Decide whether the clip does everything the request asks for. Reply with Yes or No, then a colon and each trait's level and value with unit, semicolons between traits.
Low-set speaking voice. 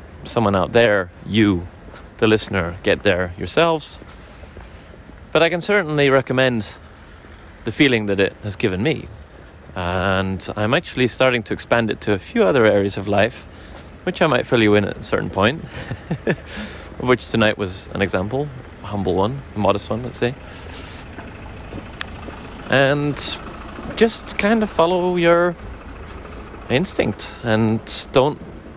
Yes: low, 105 Hz